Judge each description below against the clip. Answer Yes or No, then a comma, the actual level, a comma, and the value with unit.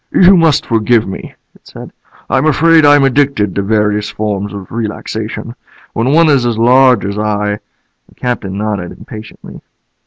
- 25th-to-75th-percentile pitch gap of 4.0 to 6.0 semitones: Yes, average, 4.6 semitones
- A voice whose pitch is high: No, low, 110 Hz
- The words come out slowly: No, average, 160 wpm